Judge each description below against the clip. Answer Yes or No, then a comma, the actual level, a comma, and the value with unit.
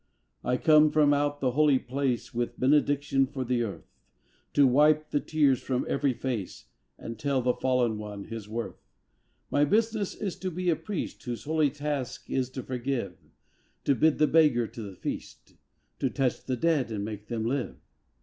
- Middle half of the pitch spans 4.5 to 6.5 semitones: No, average, 3.8 semitones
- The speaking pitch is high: No, low, 135 Hz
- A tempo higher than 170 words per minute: Yes, average, 180 wpm